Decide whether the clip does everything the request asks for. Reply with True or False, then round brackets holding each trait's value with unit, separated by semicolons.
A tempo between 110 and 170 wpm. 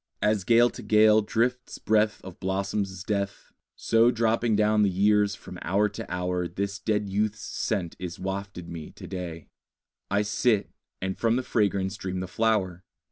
True (165 wpm)